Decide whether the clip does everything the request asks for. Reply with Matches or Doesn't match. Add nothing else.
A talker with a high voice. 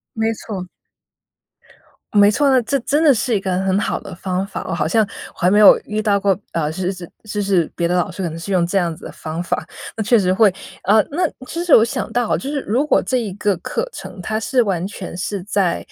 Matches